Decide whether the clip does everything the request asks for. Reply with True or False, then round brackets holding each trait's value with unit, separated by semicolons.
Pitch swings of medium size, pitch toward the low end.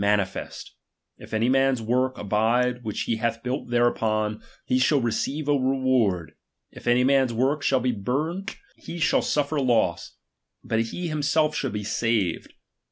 True (3.5 semitones; 125 Hz)